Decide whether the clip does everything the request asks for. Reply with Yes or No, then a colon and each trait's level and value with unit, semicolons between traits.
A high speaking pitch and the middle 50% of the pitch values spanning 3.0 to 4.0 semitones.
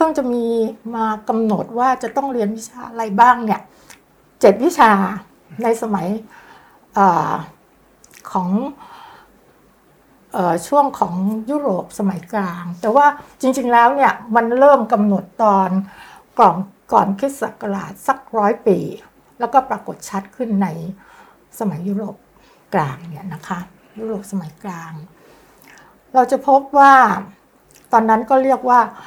No: high, 225 Hz; average, 4.6 semitones